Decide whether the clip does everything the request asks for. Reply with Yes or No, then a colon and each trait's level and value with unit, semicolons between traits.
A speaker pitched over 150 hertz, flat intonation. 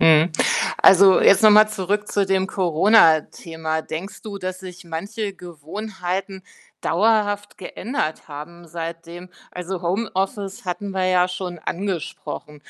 No: medium, 185 Hz; average, 3.0 semitones